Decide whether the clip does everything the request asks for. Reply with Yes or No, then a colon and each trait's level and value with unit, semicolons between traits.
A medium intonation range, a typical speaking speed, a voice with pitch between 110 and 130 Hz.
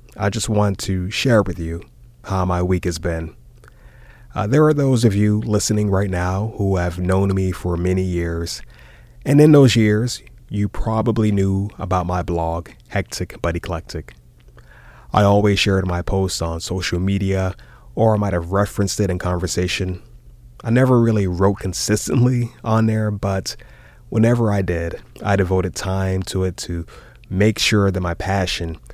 No: average, 3.1 semitones; average, 165 wpm; very low, 95 Hz